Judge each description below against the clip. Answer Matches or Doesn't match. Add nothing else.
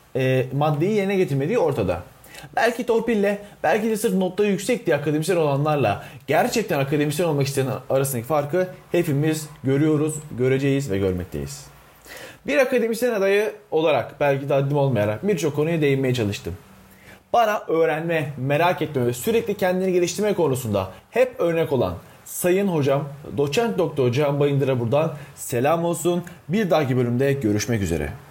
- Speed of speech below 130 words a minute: Doesn't match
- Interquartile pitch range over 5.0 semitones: Matches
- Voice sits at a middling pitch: Matches